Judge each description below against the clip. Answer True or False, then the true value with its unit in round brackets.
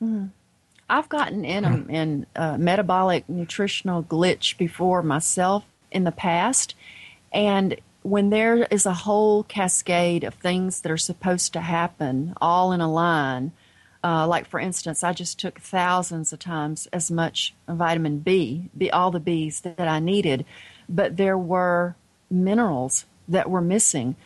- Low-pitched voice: False (175 Hz)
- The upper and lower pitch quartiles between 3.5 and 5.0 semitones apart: False (2.7 semitones)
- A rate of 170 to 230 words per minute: False (150 wpm)